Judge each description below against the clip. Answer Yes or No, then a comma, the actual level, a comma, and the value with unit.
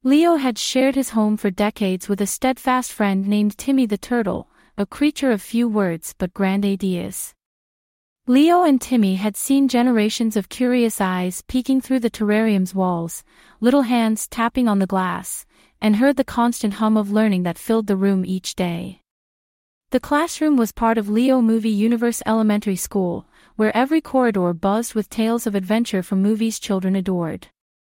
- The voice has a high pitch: Yes, high, 220 Hz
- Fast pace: No, average, 165 wpm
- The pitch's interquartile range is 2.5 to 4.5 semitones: Yes, average, 4.0 semitones